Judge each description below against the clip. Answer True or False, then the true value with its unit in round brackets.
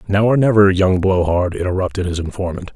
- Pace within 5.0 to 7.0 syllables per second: True (5.8 syllables/s)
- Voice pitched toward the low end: True (95 Hz)